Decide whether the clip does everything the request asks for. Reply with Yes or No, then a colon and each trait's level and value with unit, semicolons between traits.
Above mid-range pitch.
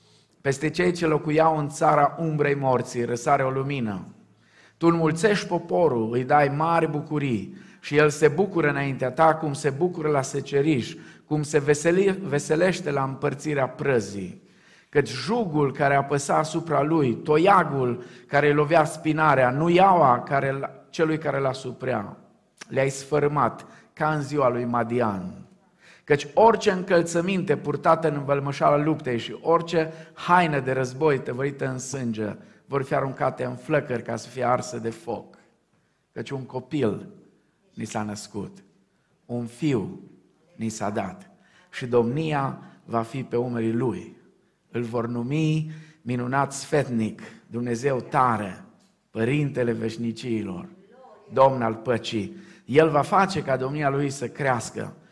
No: medium, 140 Hz